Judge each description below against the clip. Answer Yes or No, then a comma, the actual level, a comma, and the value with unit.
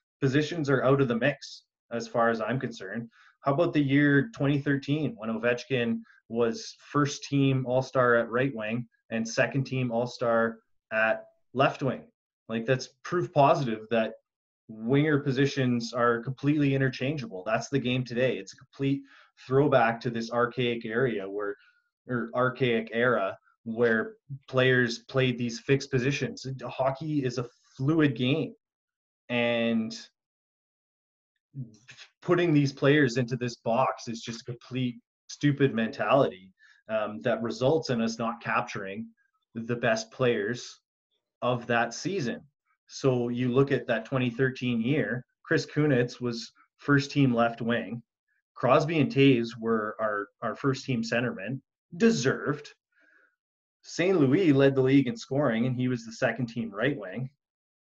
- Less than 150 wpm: Yes, average, 140 wpm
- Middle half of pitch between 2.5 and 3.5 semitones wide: Yes, average, 2.9 semitones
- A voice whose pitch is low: Yes, low, 125 Hz